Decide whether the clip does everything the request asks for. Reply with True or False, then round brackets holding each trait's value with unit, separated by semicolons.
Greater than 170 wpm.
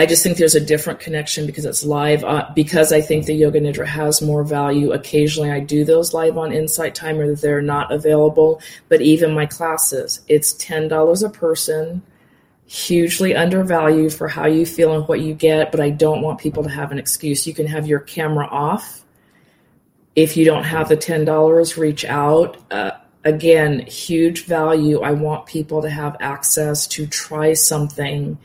True (180 wpm)